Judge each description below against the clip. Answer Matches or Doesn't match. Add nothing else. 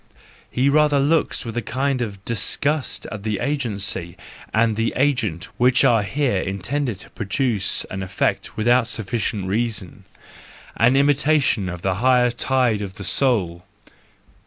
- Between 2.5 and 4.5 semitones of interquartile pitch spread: Doesn't match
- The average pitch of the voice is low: Matches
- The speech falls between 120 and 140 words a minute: Matches